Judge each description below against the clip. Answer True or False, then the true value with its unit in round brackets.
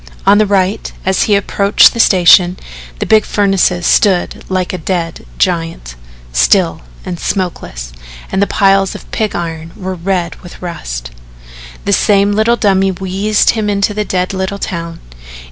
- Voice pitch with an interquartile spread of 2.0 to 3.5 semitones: True (2.5 semitones)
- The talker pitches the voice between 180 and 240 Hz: True (190 Hz)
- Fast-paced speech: False (155 wpm)